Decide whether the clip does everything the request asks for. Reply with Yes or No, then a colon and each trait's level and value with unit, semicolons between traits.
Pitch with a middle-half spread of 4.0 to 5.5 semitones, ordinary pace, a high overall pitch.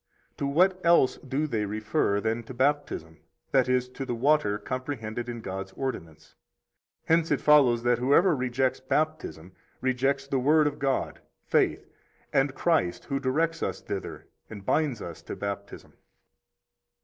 No: average, 5.0 semitones; average, 150 wpm; low, 130 Hz